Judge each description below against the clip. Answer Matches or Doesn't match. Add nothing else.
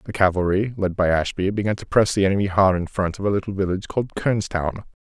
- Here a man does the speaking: Matches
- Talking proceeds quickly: Matches